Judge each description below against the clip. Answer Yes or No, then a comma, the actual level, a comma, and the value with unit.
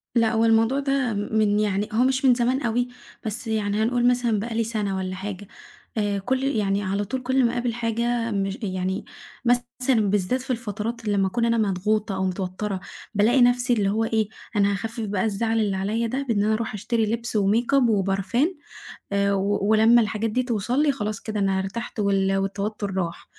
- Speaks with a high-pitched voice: Yes, high, 220 Hz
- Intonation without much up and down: No, average, 3.1 semitones